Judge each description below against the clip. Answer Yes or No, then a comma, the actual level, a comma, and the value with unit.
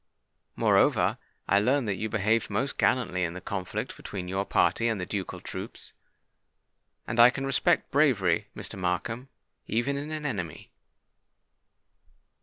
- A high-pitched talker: No, low, 110 Hz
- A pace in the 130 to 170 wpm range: Yes, average, 140 wpm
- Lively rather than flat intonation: Yes, wide, 6.2 semitones